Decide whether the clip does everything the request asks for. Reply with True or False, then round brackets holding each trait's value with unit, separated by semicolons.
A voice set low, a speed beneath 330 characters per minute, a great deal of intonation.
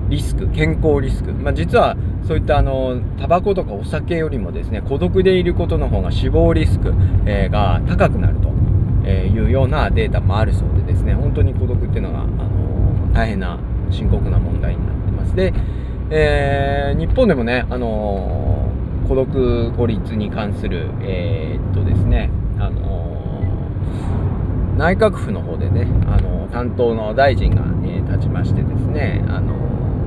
False (100 Hz; 300 characters per minute; 2.9 semitones)